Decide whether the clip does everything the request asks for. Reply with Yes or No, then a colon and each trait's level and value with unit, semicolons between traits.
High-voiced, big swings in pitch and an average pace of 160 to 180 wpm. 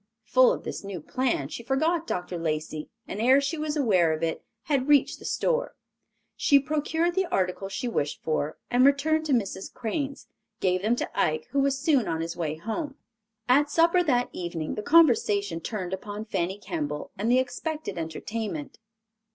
Yes: high, 230 Hz; wide, 8.1 semitones; average, 175 wpm